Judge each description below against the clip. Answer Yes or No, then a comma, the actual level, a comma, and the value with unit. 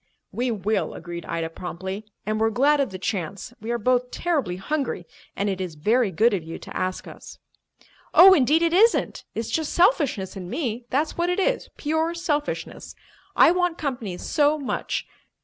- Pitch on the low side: No, high, 240 Hz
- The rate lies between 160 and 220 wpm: Yes, average, 180 wpm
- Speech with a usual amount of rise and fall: No, wide, 8.3 semitones